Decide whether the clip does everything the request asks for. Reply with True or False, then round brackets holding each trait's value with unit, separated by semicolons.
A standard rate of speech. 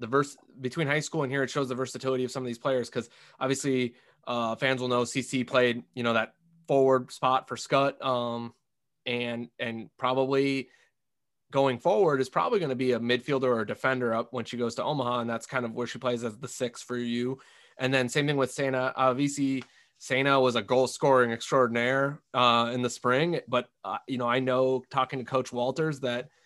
False (210 wpm)